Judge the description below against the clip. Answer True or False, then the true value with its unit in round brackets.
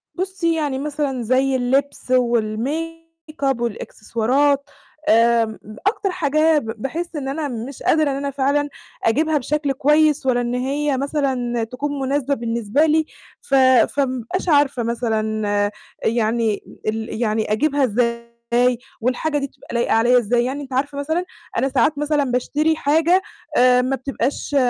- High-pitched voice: True (270 Hz)